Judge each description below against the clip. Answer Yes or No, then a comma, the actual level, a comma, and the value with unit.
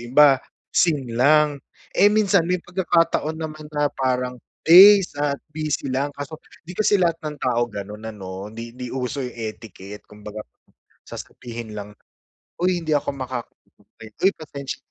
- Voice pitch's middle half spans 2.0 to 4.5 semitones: No, wide, 5.4 semitones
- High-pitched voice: No, medium, 140 Hz